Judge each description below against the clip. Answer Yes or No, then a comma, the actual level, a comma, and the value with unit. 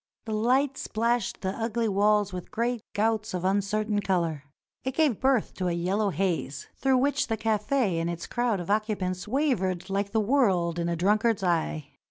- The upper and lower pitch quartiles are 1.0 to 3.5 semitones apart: No, average, 4.2 semitones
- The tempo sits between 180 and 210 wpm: Yes, average, 185 wpm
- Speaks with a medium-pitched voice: No, high, 210 Hz